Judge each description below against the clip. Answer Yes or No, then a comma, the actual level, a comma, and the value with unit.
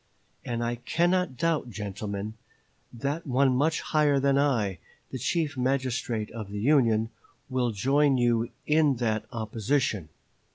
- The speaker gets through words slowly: Yes, slow, 130 wpm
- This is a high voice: No, low, 125 Hz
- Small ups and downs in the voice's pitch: No, average, 4.3 semitones